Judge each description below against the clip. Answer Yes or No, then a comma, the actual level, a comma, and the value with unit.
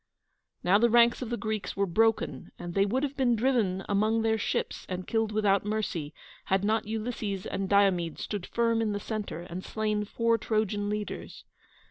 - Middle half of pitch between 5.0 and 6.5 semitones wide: No, narrow, 2.4 semitones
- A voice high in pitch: Yes, high, 215 Hz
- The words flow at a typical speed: Yes, average, 180 wpm